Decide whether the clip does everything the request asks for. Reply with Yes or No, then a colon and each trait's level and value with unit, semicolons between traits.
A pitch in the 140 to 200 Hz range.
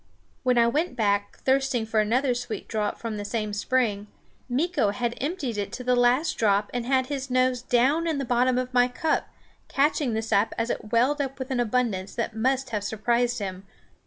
No: high, 245 Hz